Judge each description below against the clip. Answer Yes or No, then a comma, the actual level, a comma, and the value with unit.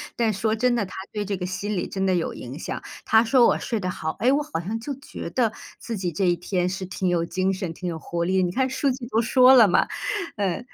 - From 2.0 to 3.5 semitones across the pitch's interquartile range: No, average, 4.7 semitones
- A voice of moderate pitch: No, high, 200 Hz